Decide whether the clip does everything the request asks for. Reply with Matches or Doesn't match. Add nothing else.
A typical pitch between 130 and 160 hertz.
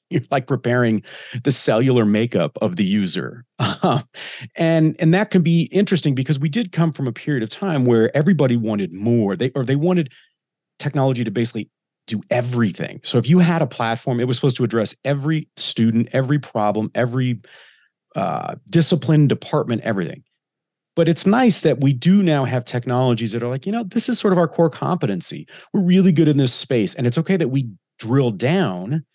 Matches